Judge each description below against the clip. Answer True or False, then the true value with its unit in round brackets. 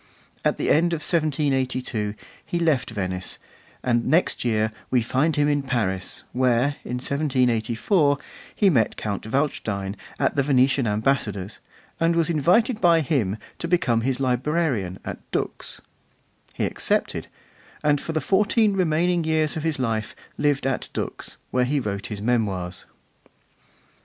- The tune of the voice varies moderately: False (5.8 semitones)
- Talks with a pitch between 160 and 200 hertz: False (135 Hz)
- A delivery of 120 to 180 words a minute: True (140 wpm)